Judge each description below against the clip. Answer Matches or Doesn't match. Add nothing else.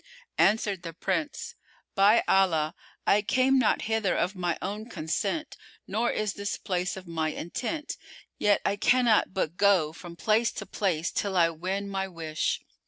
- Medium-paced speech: Matches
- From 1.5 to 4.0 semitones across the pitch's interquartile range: Matches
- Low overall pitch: Doesn't match